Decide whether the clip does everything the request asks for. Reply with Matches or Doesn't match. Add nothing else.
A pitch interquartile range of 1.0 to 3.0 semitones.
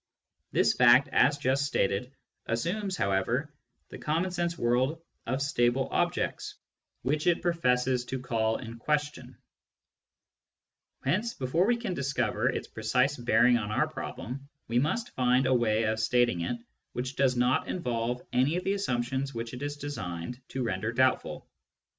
Doesn't match